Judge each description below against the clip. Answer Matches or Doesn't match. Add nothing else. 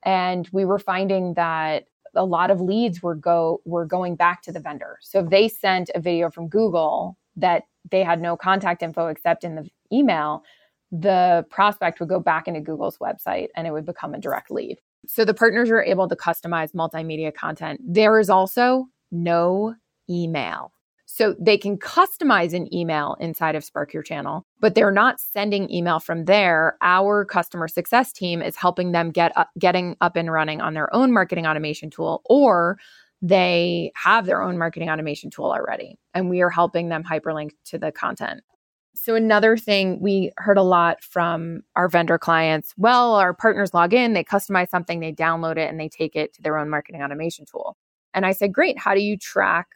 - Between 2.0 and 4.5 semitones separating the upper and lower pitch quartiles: Matches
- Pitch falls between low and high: Matches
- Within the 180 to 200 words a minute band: Matches